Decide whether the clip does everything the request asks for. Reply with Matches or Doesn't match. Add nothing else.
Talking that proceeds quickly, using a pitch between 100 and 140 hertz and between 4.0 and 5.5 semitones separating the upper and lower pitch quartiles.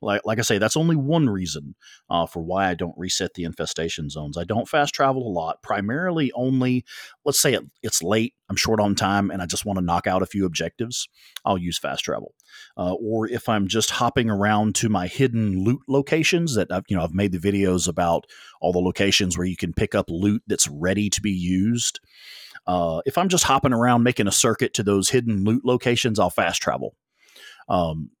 Matches